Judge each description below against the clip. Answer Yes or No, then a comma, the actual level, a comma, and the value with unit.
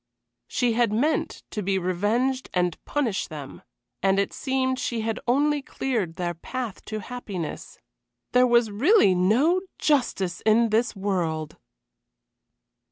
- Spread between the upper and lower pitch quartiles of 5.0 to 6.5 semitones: Yes, average, 5.3 semitones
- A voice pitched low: No, high, 220 Hz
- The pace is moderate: No, slow, 130 wpm